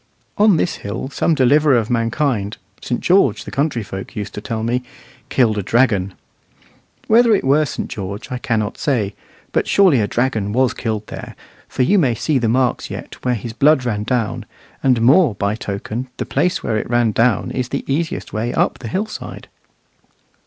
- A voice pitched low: Yes, low, 120 Hz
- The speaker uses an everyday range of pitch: Yes, average, 4.3 semitones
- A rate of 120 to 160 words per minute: No, average, 185 wpm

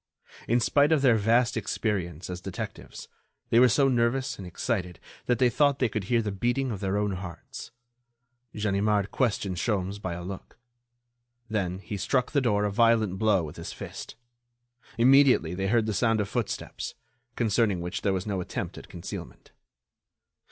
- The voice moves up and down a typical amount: Yes, average, 3.9 semitones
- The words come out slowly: No, average, 170 wpm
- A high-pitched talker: No, low, 105 Hz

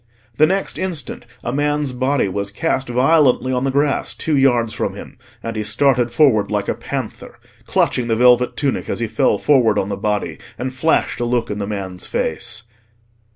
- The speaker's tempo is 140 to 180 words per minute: No, average, 190 wpm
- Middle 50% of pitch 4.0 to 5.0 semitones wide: Yes, average, 4.5 semitones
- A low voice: Yes, low, 125 Hz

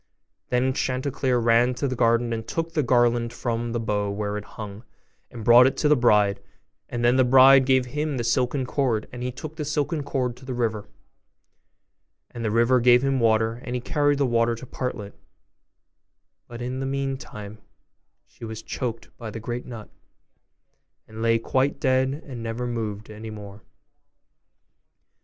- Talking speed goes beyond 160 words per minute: Yes, average, 175 wpm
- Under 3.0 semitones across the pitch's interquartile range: Yes, narrow, 2.5 semitones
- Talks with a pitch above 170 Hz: No, low, 120 Hz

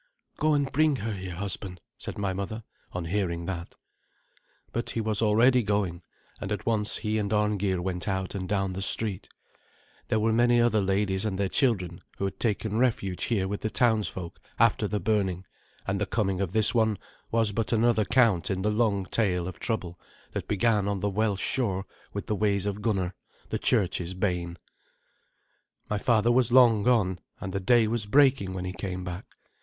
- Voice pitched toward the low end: Yes, low, 105 Hz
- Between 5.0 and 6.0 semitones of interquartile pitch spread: No, average, 3.0 semitones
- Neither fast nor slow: Yes, average, 185 wpm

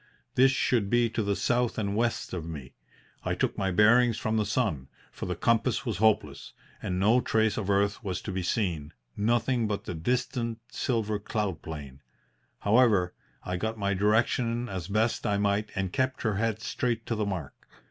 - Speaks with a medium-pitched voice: No, low, 105 Hz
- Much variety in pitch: No, average, 3.4 semitones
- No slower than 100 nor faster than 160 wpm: No, average, 185 wpm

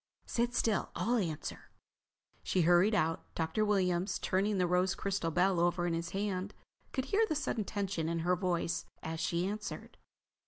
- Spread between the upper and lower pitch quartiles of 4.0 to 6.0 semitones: No, average, 3.3 semitones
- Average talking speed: Yes, average, 165 wpm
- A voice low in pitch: No, medium, 185 Hz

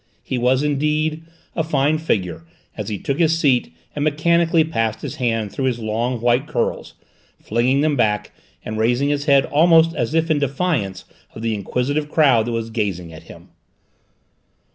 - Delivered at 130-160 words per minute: No, average, 170 wpm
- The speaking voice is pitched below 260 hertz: Yes, low, 135 Hz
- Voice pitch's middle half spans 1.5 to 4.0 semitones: No, average, 5.2 semitones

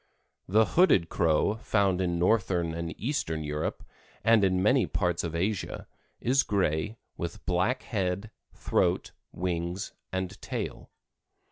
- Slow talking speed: Yes, slow, 125 wpm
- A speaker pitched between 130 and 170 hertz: No, very low, 95 Hz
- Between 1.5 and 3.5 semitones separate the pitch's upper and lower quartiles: No, average, 3.9 semitones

